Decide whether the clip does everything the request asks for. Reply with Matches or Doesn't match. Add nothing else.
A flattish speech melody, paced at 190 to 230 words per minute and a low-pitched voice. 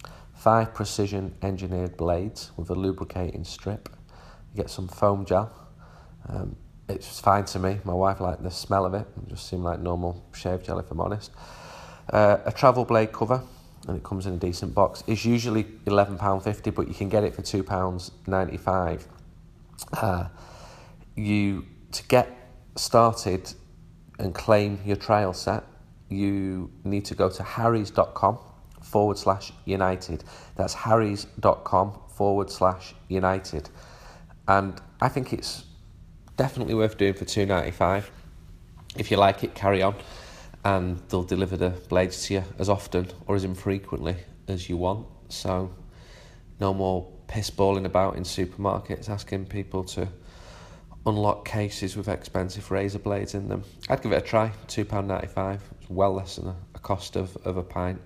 Doesn't match